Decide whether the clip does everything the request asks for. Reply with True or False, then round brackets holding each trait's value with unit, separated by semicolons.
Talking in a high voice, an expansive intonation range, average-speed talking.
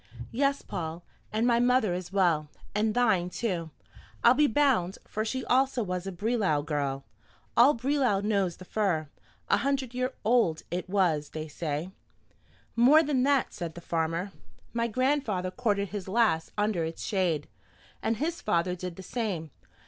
True (200 Hz; 6.0 semitones; 160 wpm)